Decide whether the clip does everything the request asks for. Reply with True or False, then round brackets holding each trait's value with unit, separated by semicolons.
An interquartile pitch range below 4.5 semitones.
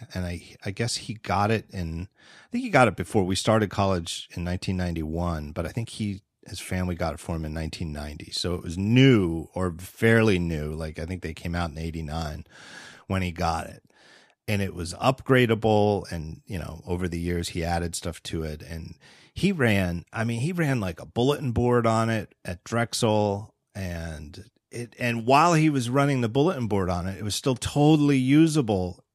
False (5.5 semitones)